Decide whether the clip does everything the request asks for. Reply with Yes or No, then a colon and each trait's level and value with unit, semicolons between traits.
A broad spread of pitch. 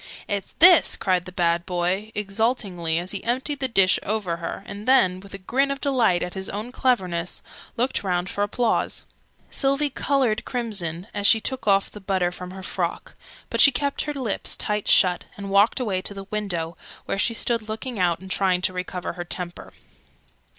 No: average, 4.6 semitones